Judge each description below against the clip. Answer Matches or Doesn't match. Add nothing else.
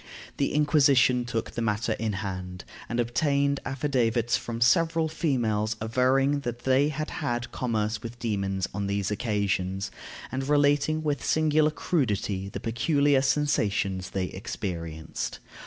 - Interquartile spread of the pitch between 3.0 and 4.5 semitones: Doesn't match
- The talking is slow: Matches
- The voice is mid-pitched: Doesn't match